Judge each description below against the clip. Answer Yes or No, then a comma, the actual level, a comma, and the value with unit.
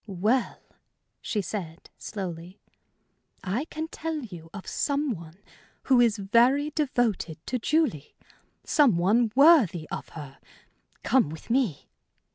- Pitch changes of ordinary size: No, wide, 7.7 semitones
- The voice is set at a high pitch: Yes, high, 220 Hz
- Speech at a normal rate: No, slow, 120 wpm